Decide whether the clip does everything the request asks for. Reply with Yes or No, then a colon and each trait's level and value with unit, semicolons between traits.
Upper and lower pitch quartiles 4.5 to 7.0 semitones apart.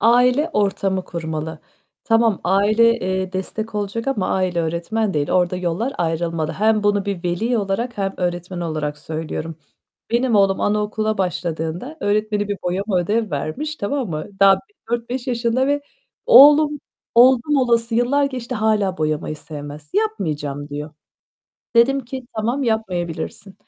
Yes: average, 5.2 semitones